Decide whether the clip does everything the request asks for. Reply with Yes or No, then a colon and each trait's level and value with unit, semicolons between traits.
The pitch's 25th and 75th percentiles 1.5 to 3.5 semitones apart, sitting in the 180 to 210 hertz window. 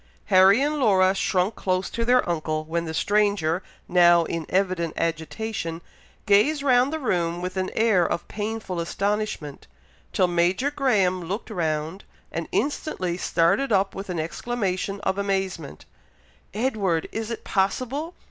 No: average, 4.3 semitones; high, 190 Hz